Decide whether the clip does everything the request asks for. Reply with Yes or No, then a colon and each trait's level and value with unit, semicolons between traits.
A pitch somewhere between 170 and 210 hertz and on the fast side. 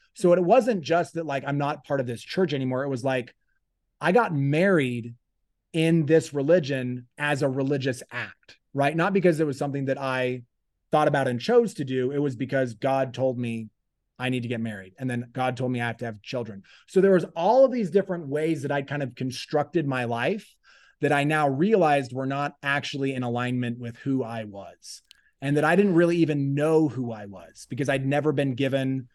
No: medium, 140 Hz; fast, 215 wpm